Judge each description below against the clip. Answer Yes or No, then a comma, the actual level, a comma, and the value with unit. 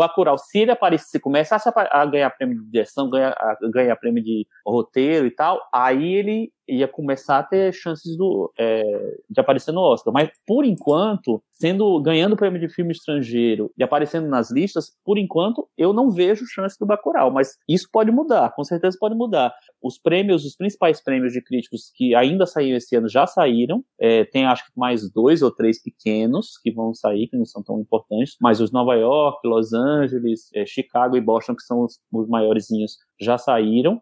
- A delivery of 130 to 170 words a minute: No, fast, 185 wpm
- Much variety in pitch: Yes, wide, 7.6 semitones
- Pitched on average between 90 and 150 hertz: Yes, medium, 140 Hz